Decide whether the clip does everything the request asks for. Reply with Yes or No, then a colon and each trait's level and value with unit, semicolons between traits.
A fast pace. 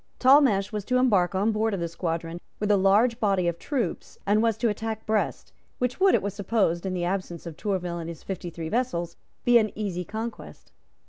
Yes: fast, 210 wpm